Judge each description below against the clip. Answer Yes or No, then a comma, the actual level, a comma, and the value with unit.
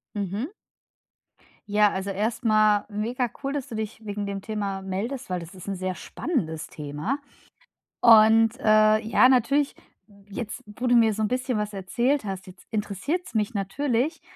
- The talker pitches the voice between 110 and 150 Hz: No, high, 215 Hz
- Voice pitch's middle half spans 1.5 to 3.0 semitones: No, average, 3.6 semitones